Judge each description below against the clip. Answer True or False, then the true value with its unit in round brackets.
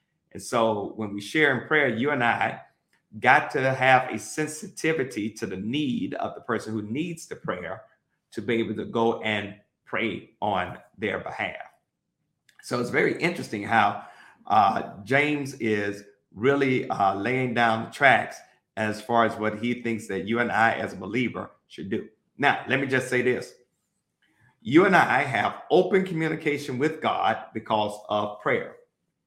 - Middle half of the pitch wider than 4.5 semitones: True (5.2 semitones)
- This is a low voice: True (120 Hz)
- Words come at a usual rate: True (165 wpm)